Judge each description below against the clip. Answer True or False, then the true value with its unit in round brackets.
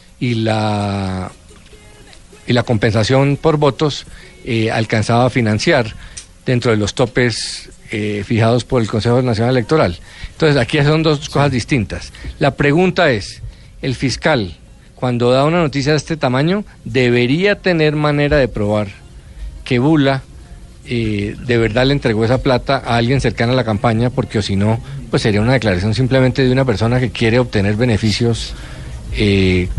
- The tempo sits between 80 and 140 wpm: False (155 wpm)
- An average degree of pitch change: True (4.1 semitones)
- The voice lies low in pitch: True (120 Hz)